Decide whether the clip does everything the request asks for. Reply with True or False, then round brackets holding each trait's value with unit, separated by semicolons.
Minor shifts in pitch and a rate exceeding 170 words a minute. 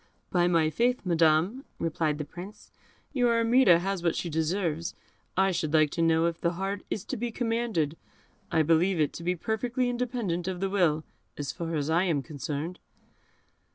False (4.2 semitones; 180 wpm)